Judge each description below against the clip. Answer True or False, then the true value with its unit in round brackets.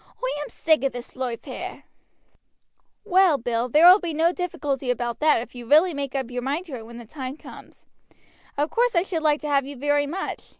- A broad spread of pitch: False (4.7 semitones)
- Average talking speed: False (220 wpm)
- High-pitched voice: True (290 Hz)